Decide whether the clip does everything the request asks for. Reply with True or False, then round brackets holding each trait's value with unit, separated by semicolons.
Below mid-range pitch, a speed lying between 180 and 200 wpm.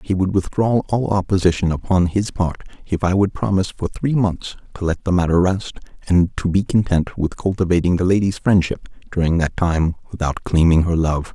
True (90 Hz; 190 wpm)